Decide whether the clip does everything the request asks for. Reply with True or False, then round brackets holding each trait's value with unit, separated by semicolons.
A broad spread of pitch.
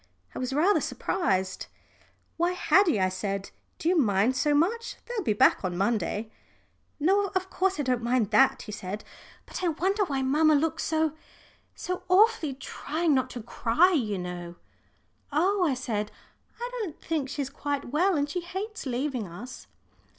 True (7.8 semitones)